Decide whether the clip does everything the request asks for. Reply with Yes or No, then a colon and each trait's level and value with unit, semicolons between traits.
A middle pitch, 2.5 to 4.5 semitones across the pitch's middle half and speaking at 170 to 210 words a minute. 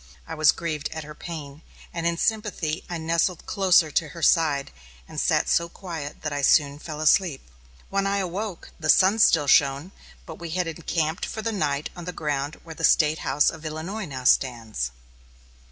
Yes: medium, 160 Hz; average, 2.9 semitones; average, 185 wpm